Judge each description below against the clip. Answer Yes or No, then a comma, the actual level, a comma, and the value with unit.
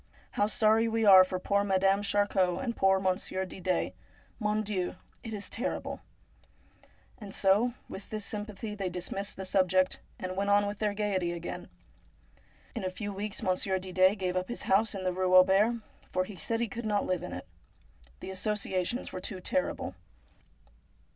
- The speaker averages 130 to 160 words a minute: No, average, 180 wpm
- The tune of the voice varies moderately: No, narrow, 2.3 semitones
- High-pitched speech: Yes, high, 195 Hz